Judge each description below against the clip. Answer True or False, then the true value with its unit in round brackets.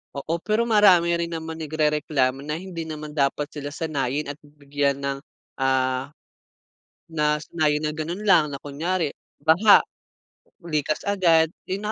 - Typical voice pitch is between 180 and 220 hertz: False (155 Hz)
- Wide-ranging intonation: False (2.8 semitones)